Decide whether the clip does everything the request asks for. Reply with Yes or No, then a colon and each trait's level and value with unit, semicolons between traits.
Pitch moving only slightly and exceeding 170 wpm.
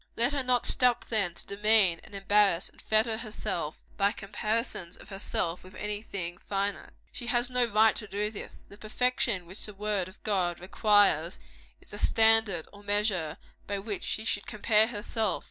Yes: narrow, 2.2 semitones; average, 180 wpm